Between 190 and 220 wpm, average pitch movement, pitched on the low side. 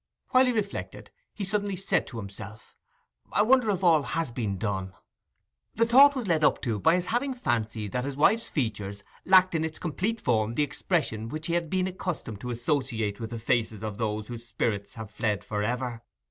No: average, 200 wpm; wide, 9.0 semitones; low, 125 Hz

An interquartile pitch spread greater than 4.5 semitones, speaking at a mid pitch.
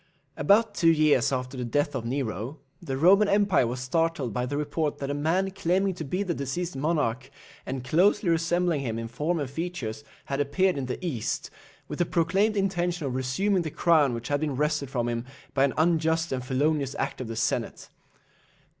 Yes: average, 5.0 semitones; medium, 150 Hz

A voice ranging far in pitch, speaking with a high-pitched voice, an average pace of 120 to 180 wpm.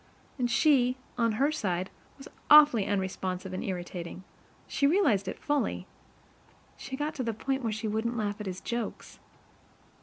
Yes: wide, 6.0 semitones; high, 230 Hz; average, 155 wpm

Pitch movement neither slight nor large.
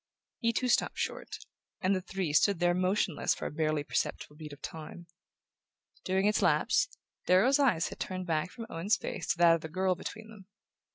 Yes: average, 3.7 semitones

